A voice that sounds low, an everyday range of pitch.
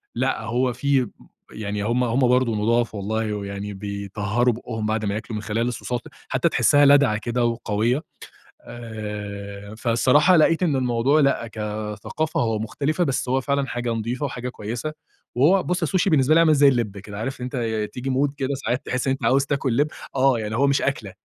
Yes: low, 120 Hz; average, 4.1 semitones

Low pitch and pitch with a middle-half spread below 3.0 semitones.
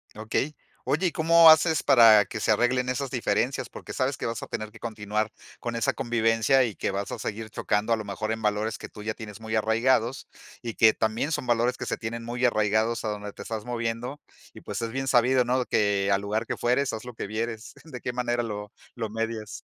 Yes: low, 115 Hz; narrow, 2.5 semitones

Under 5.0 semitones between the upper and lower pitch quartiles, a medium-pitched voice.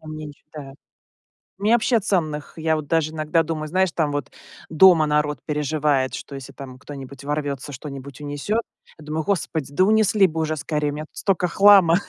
Yes: narrow, 2.6 semitones; medium, 155 Hz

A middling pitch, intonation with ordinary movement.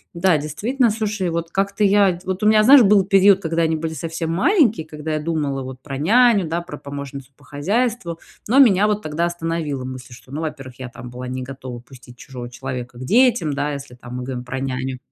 No: medium, 160 Hz; wide, 6.8 semitones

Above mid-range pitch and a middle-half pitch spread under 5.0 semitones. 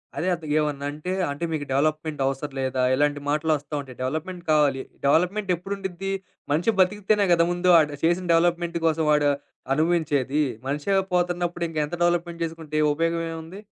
No: medium, 160 Hz; average, 3.0 semitones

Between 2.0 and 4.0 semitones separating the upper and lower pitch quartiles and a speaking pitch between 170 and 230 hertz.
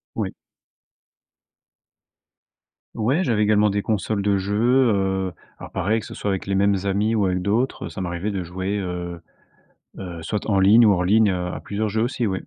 No: narrow, 2.5 semitones; low, 100 Hz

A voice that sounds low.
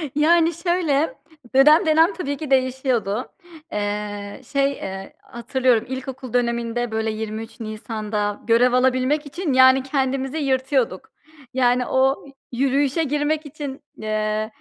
No: very high, 260 Hz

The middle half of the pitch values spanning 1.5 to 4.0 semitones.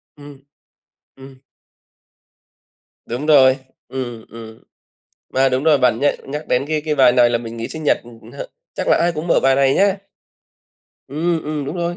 Yes: average, 3.7 semitones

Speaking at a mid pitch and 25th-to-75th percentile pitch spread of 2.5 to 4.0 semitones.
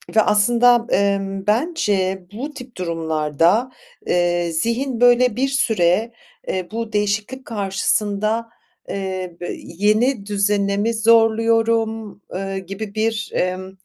No: high, 210 Hz; average, 3.3 semitones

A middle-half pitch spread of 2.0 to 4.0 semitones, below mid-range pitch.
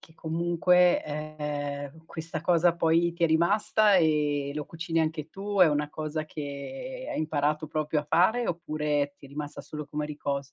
No: narrow, 2.5 semitones; medium, 155 Hz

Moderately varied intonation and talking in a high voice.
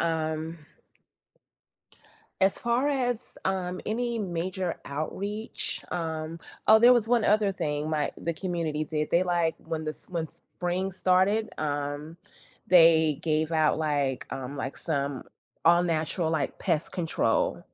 No: average, 3.5 semitones; medium, 165 Hz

